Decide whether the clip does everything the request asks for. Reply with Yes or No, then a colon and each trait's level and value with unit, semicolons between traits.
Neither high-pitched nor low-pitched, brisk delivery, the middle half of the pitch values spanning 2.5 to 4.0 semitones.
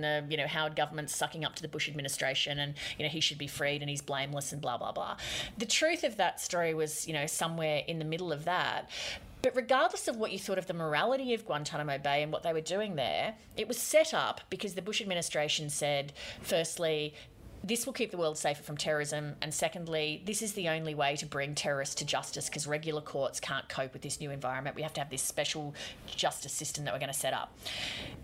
Yes: medium, 150 Hz; fast, 235 wpm; average, 3.4 semitones